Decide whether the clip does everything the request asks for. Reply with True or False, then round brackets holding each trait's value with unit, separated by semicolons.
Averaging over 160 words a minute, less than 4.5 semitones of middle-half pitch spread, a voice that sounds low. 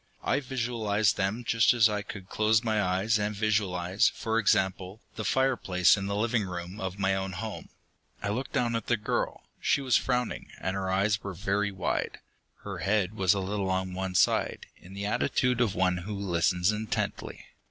True (185 wpm; 2.7 semitones; 100 Hz)